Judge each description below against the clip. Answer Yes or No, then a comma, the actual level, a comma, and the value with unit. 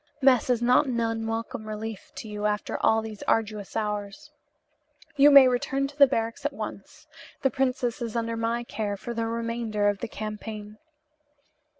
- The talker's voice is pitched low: No, high, 230 Hz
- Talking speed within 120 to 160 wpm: No, average, 170 wpm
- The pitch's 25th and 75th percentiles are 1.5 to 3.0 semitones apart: Yes, average, 2.7 semitones